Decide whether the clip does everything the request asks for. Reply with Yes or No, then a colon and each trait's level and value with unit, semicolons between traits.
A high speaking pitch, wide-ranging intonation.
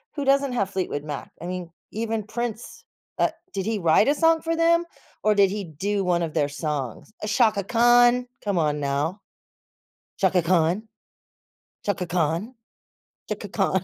Yes: high, 200 Hz; wide, 6.1 semitones